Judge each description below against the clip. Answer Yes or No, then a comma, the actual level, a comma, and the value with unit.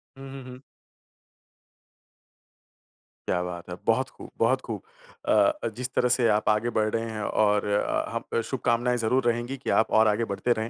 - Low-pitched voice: Yes, low, 115 Hz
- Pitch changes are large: No, average, 2.8 semitones